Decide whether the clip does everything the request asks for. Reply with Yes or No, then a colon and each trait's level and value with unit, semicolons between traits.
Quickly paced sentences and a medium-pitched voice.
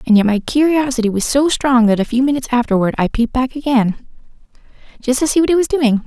No: fast, 225 wpm; very high, 255 Hz